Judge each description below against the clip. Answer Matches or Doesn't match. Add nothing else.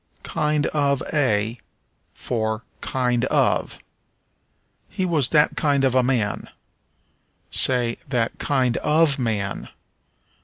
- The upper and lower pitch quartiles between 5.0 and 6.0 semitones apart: Doesn't match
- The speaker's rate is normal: Doesn't match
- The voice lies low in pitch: Matches